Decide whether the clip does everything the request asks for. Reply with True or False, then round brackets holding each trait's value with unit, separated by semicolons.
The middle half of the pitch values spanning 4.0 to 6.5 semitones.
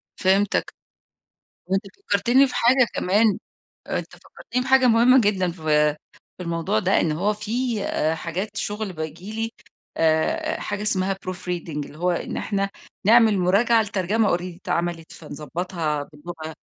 True (4.6 semitones)